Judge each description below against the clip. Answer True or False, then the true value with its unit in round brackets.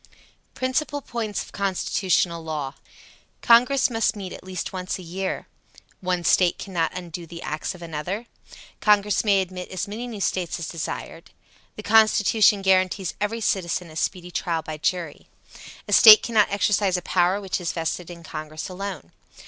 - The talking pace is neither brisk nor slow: True (160 wpm)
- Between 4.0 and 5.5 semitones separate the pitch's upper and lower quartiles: False (3.4 semitones)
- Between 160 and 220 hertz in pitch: True (185 Hz)